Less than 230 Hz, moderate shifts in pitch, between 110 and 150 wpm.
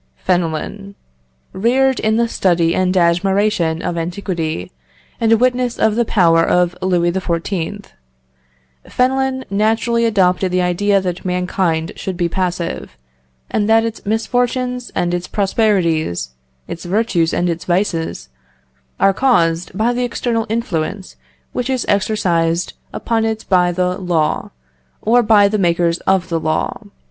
Yes: high, 190 Hz; average, 4.5 semitones; slow, 135 wpm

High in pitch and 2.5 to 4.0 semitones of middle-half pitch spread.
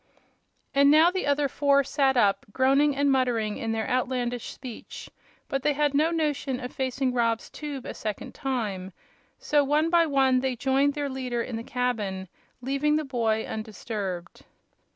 Yes: very high, 260 Hz; average, 3.6 semitones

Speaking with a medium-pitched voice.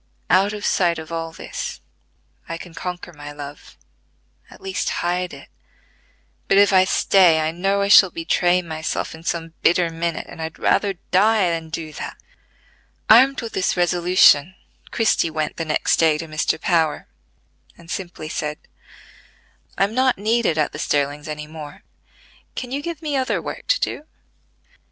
Yes: medium, 175 Hz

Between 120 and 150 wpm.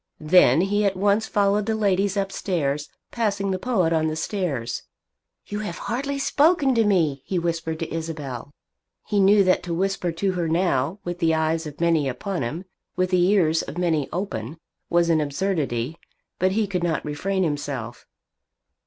No: average, 170 wpm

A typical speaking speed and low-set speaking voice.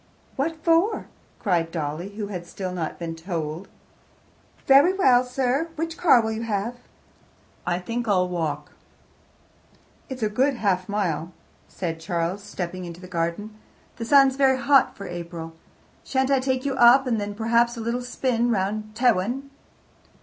No: average, 155 wpm; high, 215 Hz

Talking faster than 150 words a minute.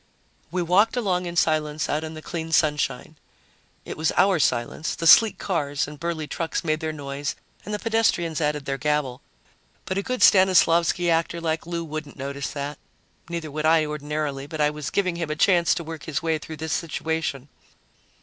Yes: average, 190 wpm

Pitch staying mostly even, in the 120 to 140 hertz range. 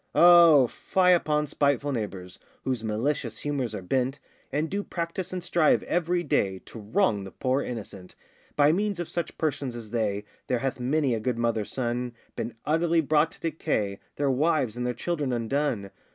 No: wide, 5.5 semitones; low, 135 Hz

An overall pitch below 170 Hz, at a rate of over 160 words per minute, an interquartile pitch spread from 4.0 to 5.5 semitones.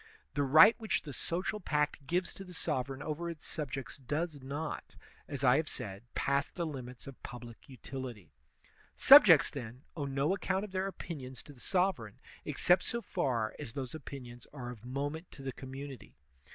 Yes: medium, 140 Hz; average, 175 wpm; average, 4.3 semitones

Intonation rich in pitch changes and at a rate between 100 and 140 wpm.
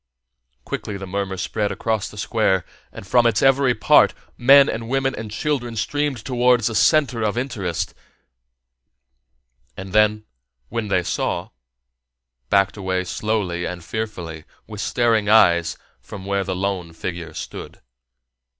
No: average, 4.0 semitones; slow, 135 wpm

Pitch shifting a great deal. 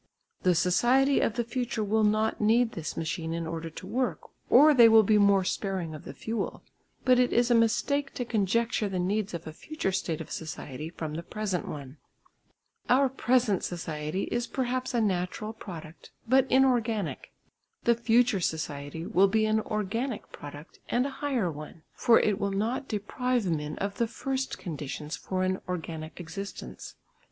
Yes: wide, 6.1 semitones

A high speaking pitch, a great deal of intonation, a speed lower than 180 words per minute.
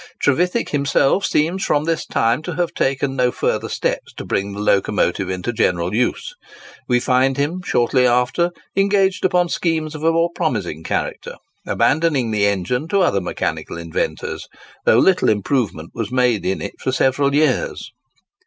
No: low, 130 Hz; wide, 7.5 semitones; average, 160 wpm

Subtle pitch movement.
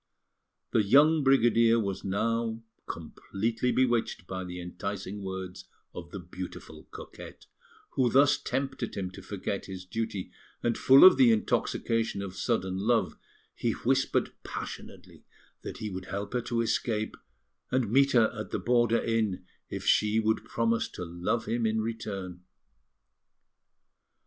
No: average, 3.6 semitones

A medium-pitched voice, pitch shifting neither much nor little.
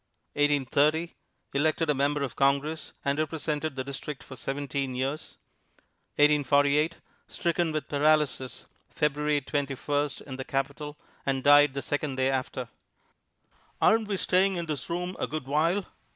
No: medium, 145 Hz; narrow, 2.1 semitones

